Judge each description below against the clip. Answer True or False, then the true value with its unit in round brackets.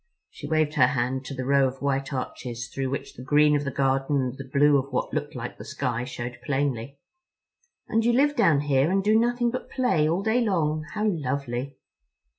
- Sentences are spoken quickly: True (210 wpm)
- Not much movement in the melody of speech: False (3.6 semitones)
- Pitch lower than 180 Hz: True (140 Hz)